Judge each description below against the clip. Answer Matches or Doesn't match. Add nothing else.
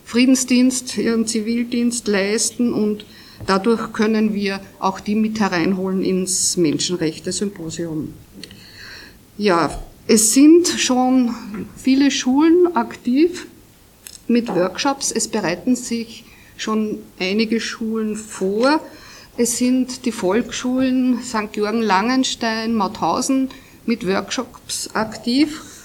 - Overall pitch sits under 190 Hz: Doesn't match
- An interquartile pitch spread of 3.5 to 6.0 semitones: Matches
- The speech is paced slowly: Matches